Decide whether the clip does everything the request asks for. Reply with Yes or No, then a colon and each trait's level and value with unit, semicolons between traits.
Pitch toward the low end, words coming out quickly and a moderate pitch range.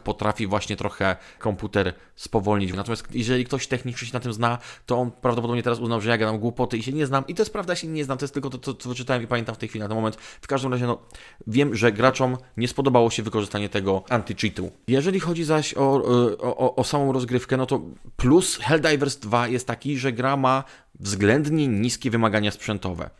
Yes: low, 120 Hz; fast, 220 wpm; average, 3.7 semitones